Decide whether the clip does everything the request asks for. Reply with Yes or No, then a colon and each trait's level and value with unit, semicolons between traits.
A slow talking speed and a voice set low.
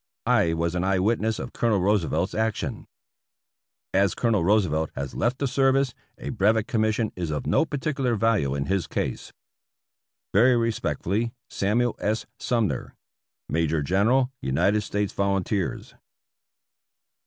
Yes: slow, 130 wpm; low, 105 Hz